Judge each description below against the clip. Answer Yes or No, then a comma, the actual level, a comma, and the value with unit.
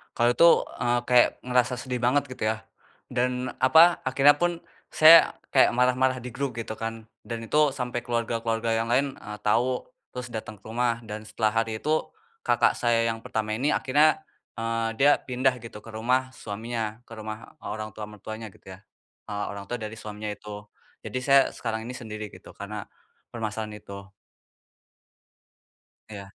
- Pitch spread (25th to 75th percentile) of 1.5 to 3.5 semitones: Yes, average, 2.7 semitones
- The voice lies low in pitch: Yes, low, 115 Hz